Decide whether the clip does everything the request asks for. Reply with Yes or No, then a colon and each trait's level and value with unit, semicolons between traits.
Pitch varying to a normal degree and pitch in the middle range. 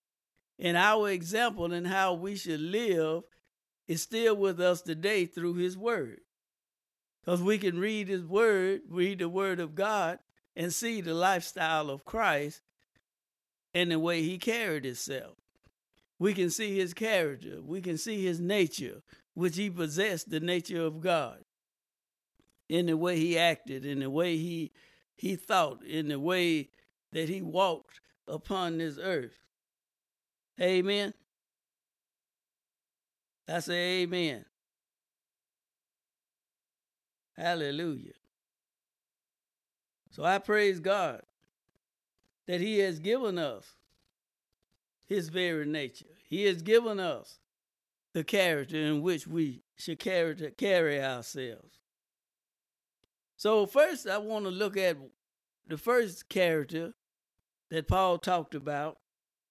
Yes: average, 3.4 semitones; medium, 180 Hz